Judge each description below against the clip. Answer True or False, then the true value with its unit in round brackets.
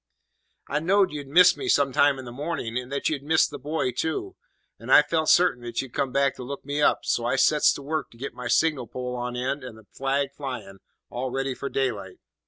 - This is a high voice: False (135 Hz)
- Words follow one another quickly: True (235 wpm)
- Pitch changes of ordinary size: True (3.1 semitones)